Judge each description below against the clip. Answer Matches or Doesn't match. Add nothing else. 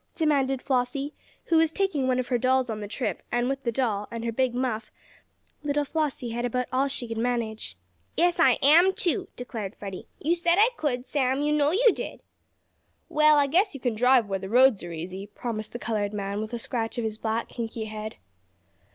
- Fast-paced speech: Matches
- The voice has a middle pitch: Doesn't match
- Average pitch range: Matches